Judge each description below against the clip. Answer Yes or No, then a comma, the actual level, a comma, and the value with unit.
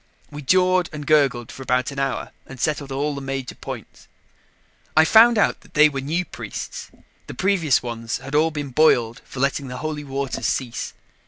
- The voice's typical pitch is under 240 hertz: Yes, medium, 140 Hz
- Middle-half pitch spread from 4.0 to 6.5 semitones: No, average, 2.8 semitones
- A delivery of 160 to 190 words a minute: Yes, average, 185 wpm